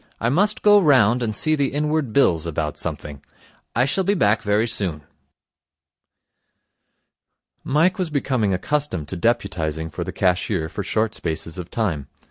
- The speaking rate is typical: Yes, average, 150 wpm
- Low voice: Yes, low, 110 Hz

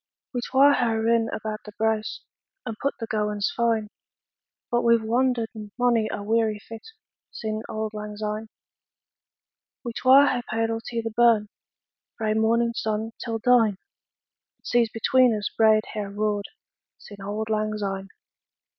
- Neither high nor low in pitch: No, high, 220 Hz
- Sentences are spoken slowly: No, average, 155 wpm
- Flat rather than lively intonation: Yes, narrow, 1.6 semitones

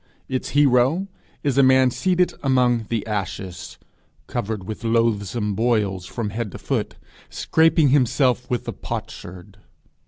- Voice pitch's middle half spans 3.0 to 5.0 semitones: Yes, average, 4.1 semitones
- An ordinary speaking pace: No, slow, 130 wpm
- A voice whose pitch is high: No, low, 120 Hz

